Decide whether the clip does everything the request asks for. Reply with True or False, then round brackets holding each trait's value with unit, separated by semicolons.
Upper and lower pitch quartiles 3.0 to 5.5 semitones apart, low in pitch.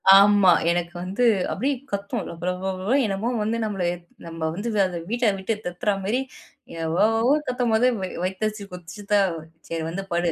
False (3.6 semitones; 195 Hz)